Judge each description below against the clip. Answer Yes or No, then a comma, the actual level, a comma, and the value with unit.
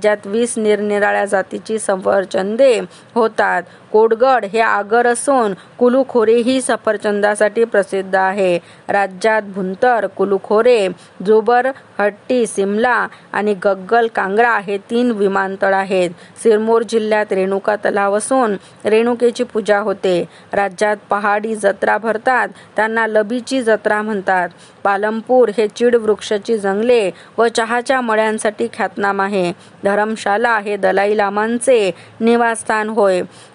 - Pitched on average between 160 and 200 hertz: No, high, 215 Hz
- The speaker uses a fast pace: No, average, 105 wpm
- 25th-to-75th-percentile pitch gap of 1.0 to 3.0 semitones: Yes, narrow, 2.6 semitones